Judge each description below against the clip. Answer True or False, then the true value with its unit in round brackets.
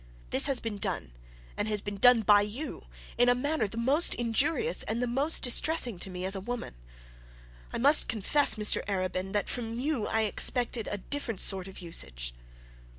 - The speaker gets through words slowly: False (170 wpm)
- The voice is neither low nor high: False (225 Hz)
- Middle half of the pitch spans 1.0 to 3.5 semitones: False (3.9 semitones)